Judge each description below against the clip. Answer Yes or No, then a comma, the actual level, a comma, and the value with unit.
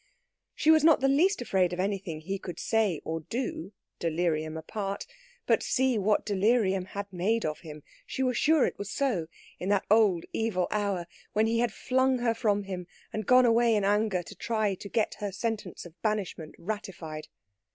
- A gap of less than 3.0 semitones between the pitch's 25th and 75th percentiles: No, average, 4.2 semitones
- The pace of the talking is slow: No, average, 185 wpm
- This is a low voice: No, high, 205 Hz